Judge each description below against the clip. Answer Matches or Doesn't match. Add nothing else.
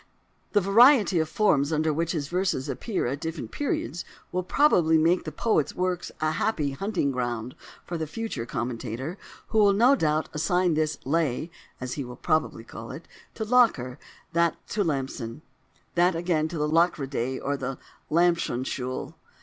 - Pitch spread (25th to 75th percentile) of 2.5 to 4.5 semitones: Doesn't match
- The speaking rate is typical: Matches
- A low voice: Doesn't match